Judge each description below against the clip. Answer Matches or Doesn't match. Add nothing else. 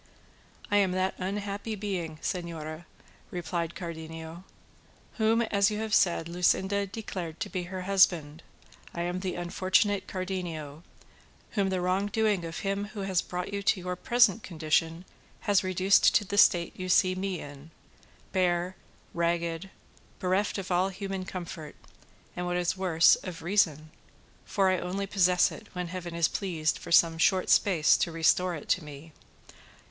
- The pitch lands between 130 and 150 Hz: Doesn't match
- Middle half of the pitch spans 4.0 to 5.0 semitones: Doesn't match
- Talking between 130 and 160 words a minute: Matches